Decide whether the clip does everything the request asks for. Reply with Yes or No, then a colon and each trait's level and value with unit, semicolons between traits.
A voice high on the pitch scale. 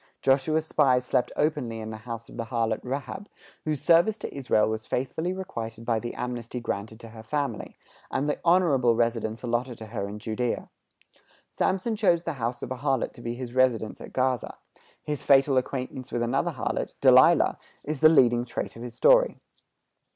No: low, 125 Hz